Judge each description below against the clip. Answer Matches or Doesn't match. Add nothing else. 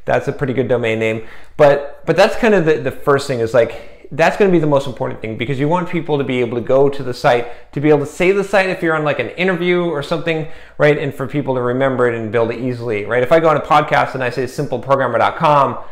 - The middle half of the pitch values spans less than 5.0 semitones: Matches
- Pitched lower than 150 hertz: Matches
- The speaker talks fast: Matches